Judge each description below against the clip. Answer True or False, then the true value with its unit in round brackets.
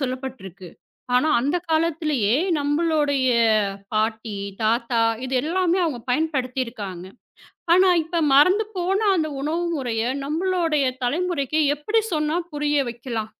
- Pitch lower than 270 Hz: False (290 Hz)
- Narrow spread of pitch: False (5.1 semitones)